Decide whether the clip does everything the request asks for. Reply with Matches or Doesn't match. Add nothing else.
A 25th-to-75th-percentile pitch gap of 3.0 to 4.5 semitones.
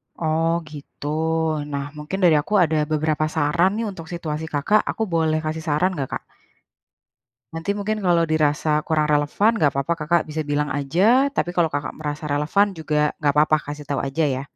Doesn't match